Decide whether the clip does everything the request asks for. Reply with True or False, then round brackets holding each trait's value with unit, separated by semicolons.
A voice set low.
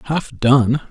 True (130 Hz)